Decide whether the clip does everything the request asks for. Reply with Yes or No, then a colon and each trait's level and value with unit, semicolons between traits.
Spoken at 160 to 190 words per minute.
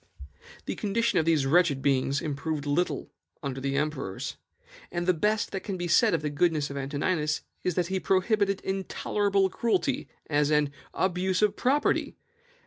Yes: average, 165 wpm